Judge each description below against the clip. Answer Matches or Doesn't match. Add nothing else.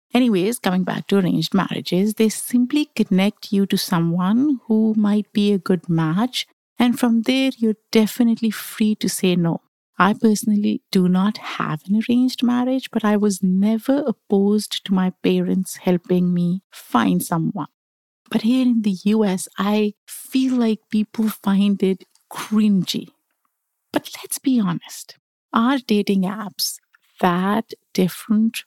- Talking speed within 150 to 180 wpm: Doesn't match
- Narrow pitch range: Doesn't match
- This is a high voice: Matches